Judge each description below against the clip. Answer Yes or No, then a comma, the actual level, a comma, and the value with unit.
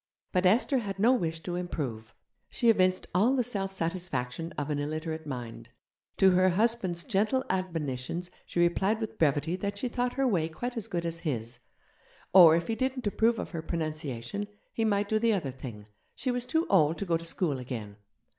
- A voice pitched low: No, medium, 180 Hz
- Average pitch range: No, wide, 5.7 semitones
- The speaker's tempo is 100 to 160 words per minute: No, average, 195 wpm